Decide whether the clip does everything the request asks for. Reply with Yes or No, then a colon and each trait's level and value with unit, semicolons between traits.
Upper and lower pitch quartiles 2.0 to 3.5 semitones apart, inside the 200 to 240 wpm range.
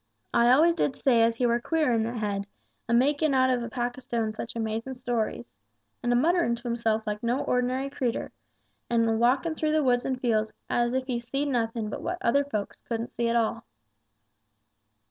Yes: narrow, 2.4 semitones; fast, 205 wpm